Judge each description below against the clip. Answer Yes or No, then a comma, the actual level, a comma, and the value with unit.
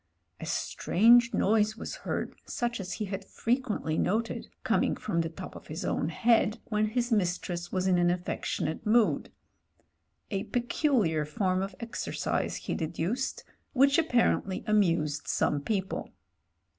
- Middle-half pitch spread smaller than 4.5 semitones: No, average, 4.9 semitones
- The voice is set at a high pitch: Yes, high, 205 Hz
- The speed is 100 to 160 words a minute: Yes, average, 145 wpm